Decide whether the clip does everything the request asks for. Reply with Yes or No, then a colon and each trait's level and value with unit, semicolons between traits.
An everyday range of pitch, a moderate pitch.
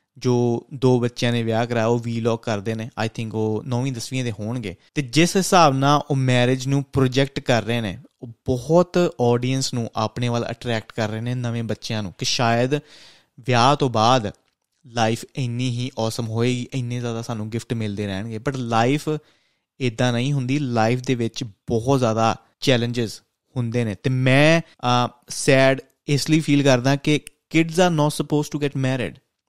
No: average, 3.1 semitones; low, 125 Hz